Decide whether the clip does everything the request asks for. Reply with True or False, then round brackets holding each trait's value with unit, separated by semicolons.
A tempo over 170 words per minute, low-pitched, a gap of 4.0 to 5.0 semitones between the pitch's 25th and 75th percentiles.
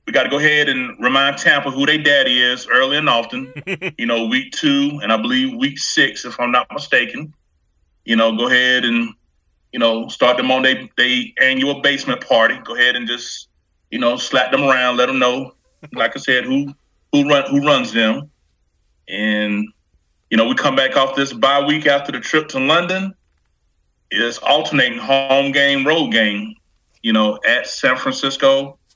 False (185 wpm; 130 Hz; 3.6 semitones)